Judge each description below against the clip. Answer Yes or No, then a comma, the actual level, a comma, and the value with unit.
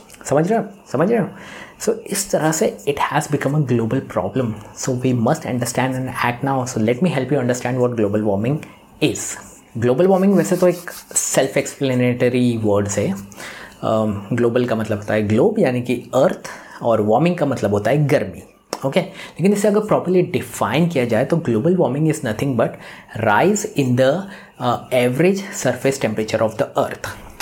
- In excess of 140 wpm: Yes, average, 185 wpm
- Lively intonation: No, average, 5.0 semitones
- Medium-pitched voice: No, low, 125 Hz